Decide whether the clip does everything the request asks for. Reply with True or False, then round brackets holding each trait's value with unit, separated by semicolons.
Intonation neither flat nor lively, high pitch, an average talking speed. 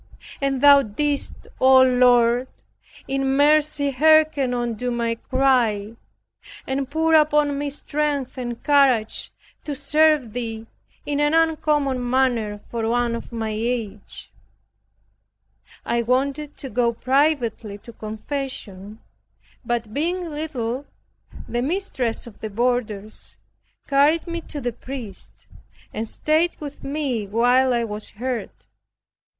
False (3.8 semitones; 255 Hz; 120 wpm)